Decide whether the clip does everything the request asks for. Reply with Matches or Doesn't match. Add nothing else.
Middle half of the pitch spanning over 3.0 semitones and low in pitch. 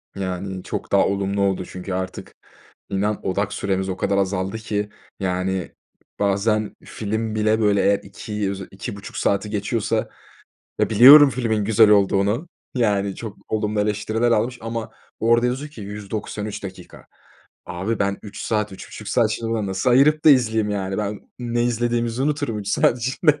Doesn't match